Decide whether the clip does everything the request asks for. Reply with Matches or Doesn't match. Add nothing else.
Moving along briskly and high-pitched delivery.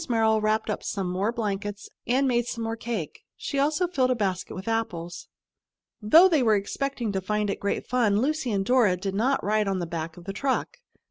Matches